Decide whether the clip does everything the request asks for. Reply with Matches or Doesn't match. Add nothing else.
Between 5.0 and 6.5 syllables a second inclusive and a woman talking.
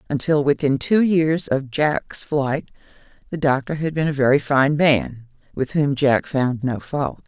Doesn't match